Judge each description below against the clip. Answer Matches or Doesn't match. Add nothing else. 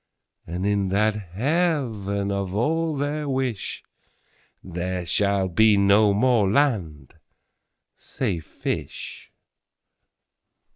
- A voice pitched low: Matches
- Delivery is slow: Matches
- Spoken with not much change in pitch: Doesn't match